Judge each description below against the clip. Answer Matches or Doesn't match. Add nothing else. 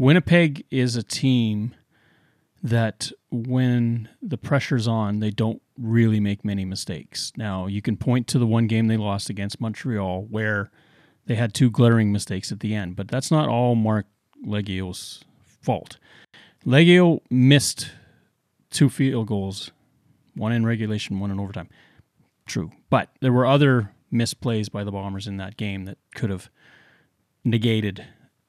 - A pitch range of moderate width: Matches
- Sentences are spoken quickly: Doesn't match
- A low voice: Matches